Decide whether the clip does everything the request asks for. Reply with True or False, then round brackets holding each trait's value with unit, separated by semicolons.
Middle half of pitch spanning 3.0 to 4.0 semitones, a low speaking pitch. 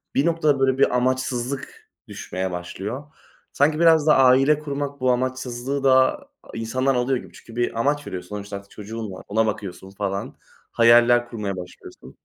False (4.4 semitones; 125 Hz)